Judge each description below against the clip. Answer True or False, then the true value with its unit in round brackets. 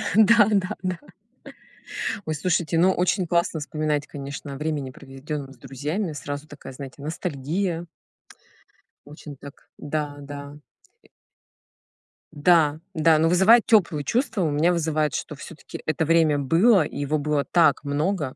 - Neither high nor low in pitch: True (155 Hz)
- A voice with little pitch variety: False (3.3 semitones)